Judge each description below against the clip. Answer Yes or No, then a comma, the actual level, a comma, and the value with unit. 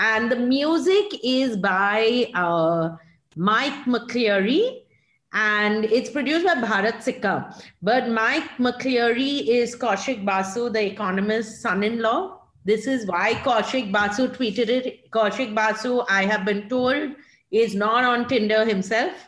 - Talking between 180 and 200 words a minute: No, slow, 135 wpm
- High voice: Yes, high, 230 Hz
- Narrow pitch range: No, average, 3.3 semitones